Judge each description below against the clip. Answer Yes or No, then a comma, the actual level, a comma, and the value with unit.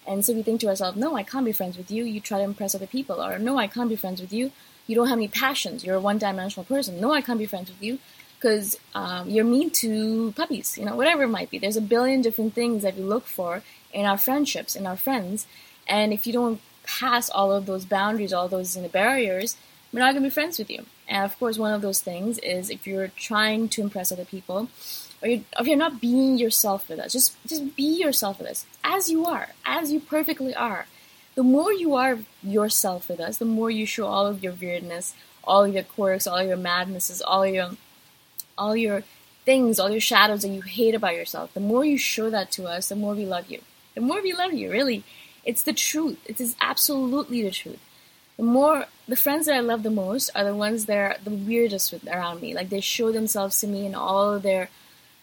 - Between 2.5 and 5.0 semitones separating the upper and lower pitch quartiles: Yes, average, 4.5 semitones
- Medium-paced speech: No, fast, 240 wpm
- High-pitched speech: Yes, high, 215 Hz